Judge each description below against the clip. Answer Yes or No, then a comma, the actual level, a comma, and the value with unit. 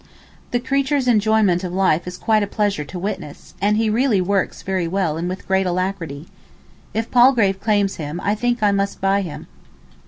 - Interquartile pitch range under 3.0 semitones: No, average, 3.3 semitones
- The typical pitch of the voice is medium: No, high, 195 Hz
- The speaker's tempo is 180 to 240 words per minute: Yes, average, 185 wpm